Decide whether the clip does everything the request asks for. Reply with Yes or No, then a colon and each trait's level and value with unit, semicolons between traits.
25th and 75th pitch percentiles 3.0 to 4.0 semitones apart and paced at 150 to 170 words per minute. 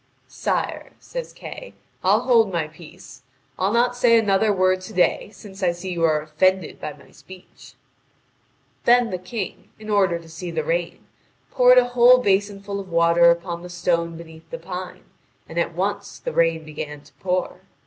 No: average, 3.5 semitones; average, 180 wpm